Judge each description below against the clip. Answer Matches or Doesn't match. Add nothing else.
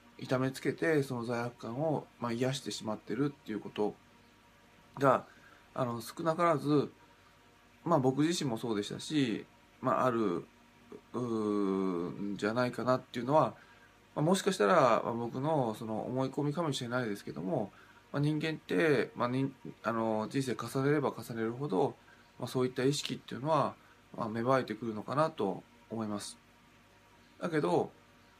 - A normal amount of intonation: Matches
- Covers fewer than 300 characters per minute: Matches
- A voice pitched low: Matches